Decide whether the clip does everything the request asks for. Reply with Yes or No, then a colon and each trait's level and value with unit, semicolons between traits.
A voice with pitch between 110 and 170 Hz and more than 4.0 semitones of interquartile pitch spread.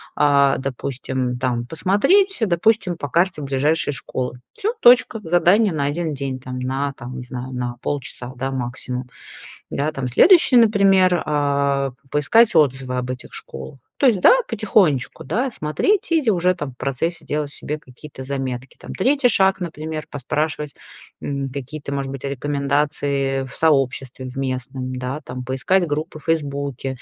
Yes: medium, 140 Hz; average, 4.7 semitones